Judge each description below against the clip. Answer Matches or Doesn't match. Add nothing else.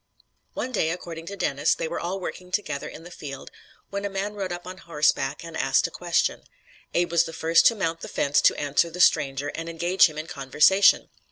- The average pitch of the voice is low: Doesn't match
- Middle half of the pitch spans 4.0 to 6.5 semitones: Doesn't match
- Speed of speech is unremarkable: Doesn't match